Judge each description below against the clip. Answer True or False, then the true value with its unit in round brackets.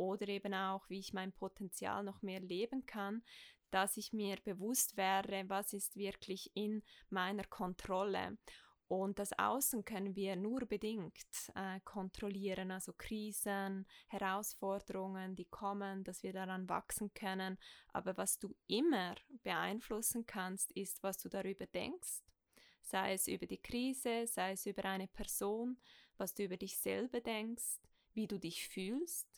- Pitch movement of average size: False (2.1 semitones)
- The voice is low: False (200 Hz)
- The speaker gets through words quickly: False (145 wpm)